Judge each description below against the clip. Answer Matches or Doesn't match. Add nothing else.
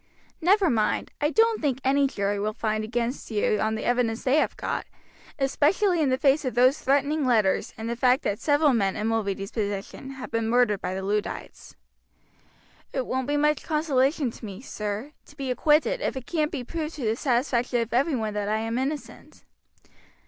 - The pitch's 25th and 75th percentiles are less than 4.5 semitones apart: Doesn't match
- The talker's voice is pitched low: Doesn't match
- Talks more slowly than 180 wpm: Doesn't match